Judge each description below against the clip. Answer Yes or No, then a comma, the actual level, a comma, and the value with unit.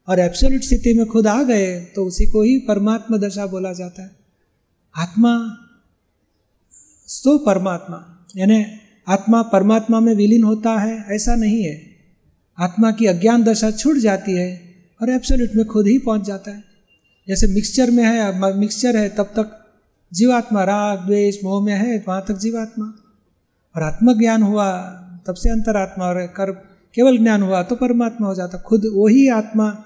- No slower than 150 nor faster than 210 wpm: Yes, average, 160 wpm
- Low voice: No, high, 210 Hz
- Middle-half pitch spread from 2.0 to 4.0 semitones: Yes, average, 2.9 semitones